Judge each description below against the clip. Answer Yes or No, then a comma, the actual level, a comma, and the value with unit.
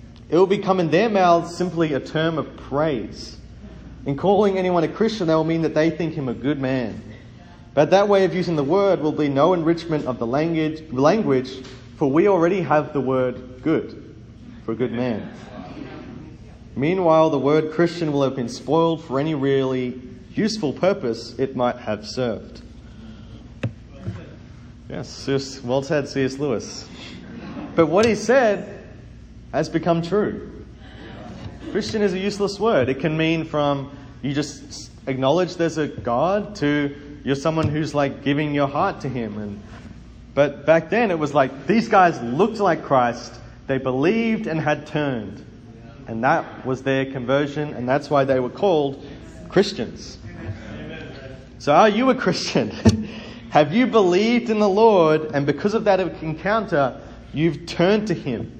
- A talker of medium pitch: Yes, medium, 150 Hz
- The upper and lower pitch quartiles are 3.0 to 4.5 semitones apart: No, average, 5.1 semitones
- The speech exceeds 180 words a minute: No, average, 160 wpm